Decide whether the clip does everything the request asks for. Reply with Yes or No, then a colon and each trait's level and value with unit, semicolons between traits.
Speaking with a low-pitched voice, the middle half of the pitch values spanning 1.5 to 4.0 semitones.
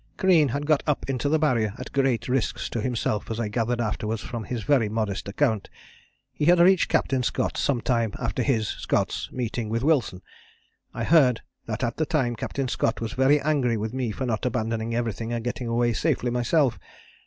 Yes: low, 120 Hz; average, 3.4 semitones